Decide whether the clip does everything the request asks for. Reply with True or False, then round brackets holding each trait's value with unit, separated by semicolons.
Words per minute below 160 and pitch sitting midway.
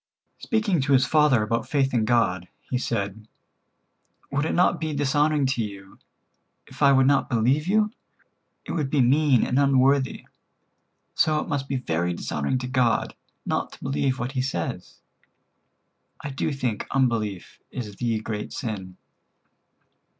False (150 wpm; 130 Hz)